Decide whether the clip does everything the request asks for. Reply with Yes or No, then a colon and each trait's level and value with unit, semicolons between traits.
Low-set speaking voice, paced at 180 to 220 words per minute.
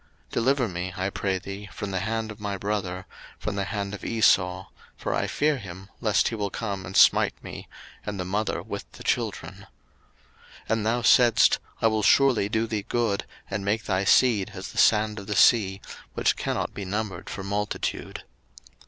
Yes: low, 105 Hz; average, 190 wpm